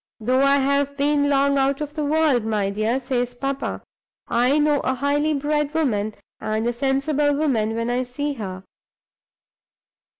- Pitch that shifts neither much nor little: Yes, average, 3.2 semitones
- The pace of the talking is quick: No, average, 160 wpm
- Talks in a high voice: Yes, very high, 275 Hz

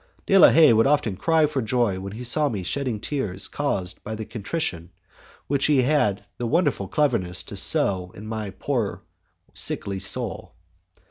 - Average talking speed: Yes, average, 175 wpm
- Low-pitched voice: Yes, low, 115 Hz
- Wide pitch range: Yes, wide, 6.5 semitones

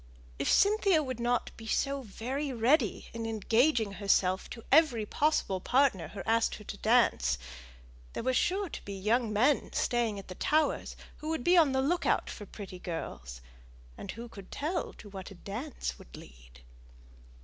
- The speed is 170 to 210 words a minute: Yes, average, 175 wpm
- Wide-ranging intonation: Yes, wide, 6.0 semitones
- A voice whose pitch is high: Yes, high, 230 Hz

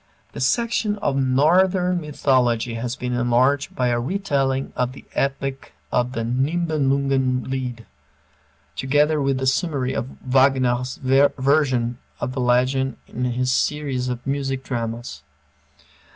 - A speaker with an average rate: No, slow, 125 wpm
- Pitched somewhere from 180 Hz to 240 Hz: No, low, 130 Hz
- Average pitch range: No, narrow, 2.1 semitones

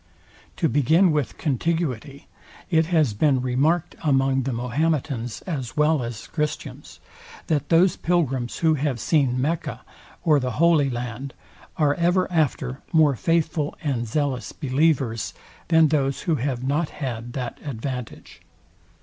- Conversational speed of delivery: No, slow, 130 wpm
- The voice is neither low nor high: Yes, medium, 145 Hz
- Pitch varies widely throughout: No, average, 4.1 semitones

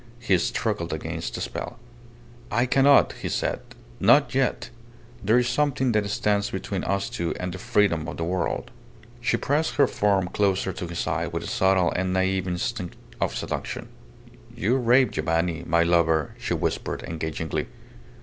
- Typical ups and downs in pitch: No, wide, 5.7 semitones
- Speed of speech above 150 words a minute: Yes, average, 160 wpm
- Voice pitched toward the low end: Yes, very low, 95 Hz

